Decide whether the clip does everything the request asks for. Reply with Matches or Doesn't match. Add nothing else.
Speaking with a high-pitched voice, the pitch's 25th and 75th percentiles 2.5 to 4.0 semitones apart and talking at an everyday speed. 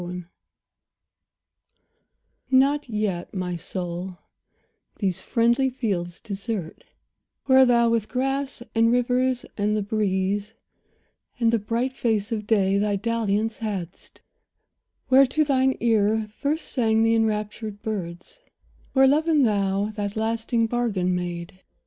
Doesn't match